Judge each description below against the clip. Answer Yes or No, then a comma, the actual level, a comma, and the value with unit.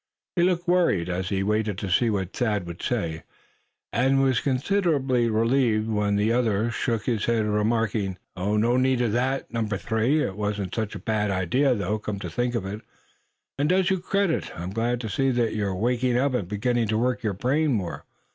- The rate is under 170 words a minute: No, average, 195 wpm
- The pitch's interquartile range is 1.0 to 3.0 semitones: No, average, 3.8 semitones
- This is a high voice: No, low, 115 Hz